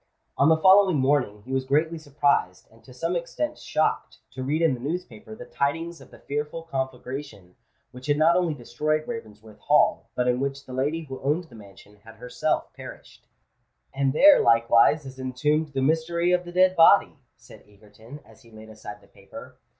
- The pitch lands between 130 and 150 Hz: Yes, medium, 140 Hz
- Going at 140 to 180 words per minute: No, average, 190 wpm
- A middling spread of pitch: Yes, average, 4.9 semitones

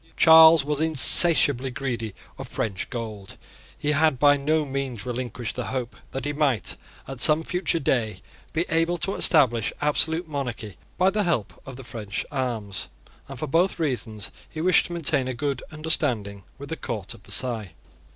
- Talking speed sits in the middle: Yes, average, 170 wpm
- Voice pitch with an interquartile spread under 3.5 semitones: No, average, 5.2 semitones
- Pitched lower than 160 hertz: Yes, low, 135 Hz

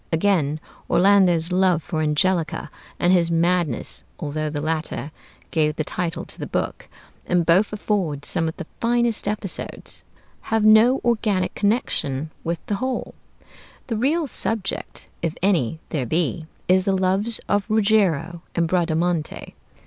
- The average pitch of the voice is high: No, medium, 180 Hz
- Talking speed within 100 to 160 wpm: Yes, average, 140 wpm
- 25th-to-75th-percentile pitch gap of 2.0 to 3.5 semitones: No, average, 4.3 semitones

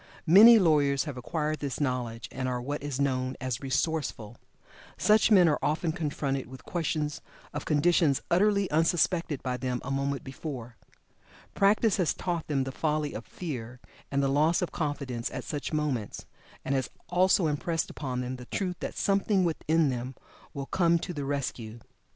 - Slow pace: No, average, 165 wpm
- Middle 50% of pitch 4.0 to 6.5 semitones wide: Yes, average, 4.3 semitones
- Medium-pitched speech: Yes, medium, 145 Hz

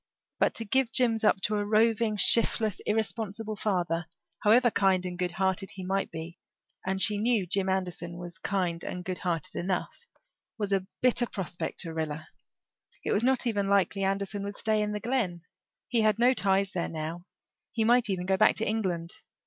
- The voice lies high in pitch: Yes, high, 195 Hz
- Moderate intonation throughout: Yes, average, 3.3 semitones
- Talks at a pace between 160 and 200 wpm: Yes, average, 185 wpm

